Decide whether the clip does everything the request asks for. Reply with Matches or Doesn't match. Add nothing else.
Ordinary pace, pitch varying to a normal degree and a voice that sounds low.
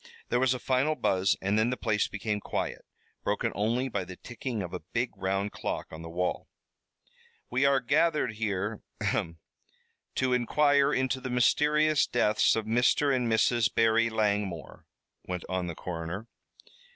Matches